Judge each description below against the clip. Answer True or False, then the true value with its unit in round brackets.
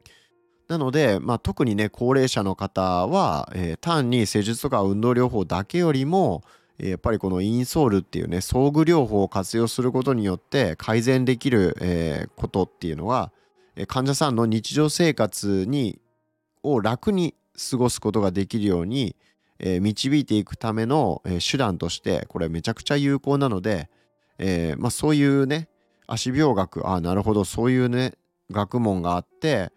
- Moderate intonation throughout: False (6.0 semitones)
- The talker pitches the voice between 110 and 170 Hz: True (115 Hz)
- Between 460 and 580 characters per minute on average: False (325 characters per minute)